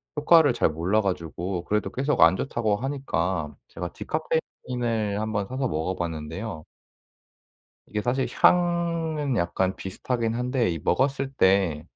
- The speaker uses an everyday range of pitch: No, wide, 6.7 semitones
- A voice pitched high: No, low, 110 Hz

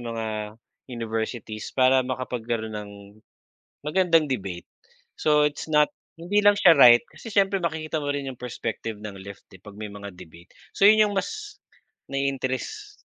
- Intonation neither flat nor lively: No, wide, 6.3 semitones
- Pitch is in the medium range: No, low, 130 Hz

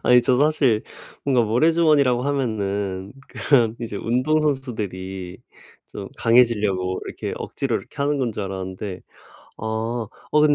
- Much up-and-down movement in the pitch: Yes, wide, 5.9 semitones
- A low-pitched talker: Yes, low, 115 Hz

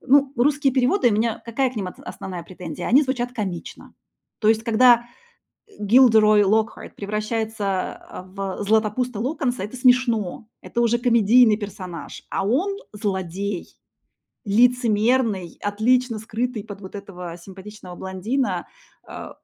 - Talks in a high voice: Yes, high, 220 Hz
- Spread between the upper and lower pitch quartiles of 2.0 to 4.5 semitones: Yes, average, 3.8 semitones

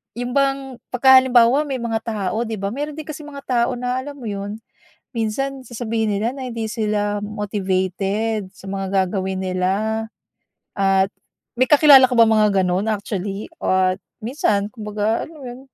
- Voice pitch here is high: Yes, high, 220 Hz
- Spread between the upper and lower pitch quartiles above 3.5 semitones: Yes, average, 4.2 semitones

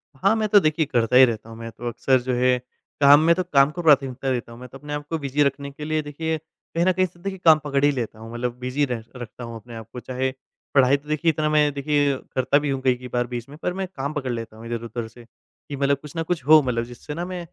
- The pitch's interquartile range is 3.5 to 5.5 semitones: Yes, average, 3.9 semitones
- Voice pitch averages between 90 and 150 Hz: Yes, medium, 140 Hz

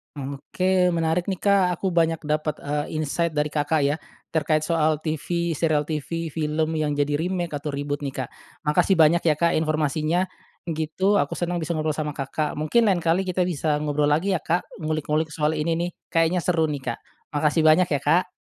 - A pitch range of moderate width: No, narrow, 2.3 semitones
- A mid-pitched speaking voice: Yes, medium, 155 Hz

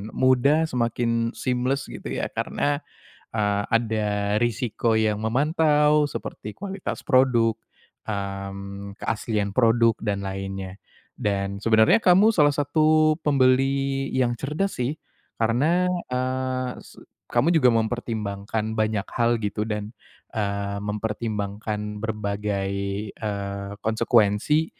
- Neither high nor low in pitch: No, low, 115 Hz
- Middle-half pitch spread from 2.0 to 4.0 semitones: No, average, 4.5 semitones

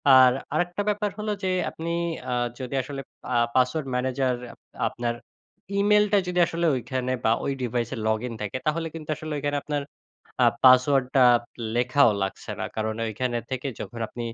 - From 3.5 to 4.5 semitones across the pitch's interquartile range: Yes, average, 4.1 semitones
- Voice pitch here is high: No, low, 130 Hz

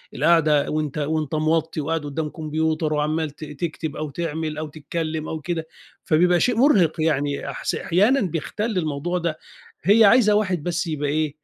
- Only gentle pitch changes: Yes, narrow, 2.3 semitones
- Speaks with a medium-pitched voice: Yes, medium, 160 Hz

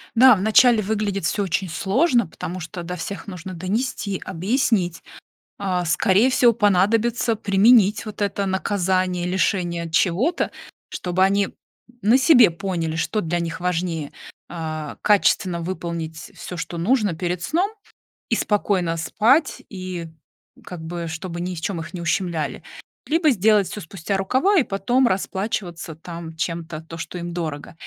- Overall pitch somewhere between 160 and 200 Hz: Yes, medium, 185 Hz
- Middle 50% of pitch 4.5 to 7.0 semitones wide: No, average, 3.9 semitones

